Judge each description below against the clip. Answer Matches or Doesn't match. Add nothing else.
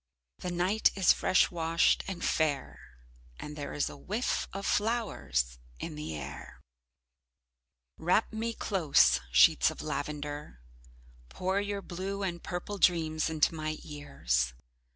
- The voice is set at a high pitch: Doesn't match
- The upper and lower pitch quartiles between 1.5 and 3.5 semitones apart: Doesn't match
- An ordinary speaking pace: Doesn't match